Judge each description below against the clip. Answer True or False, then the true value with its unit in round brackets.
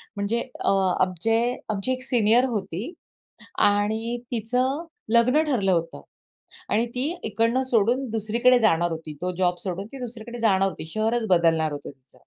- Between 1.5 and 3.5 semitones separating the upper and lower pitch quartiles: False (4.7 semitones)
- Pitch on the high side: True (220 Hz)